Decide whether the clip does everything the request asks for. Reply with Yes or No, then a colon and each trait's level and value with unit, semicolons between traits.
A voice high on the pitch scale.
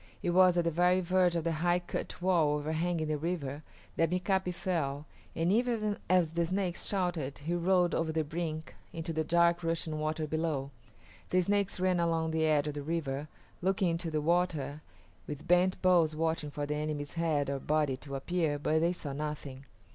No: medium, 165 Hz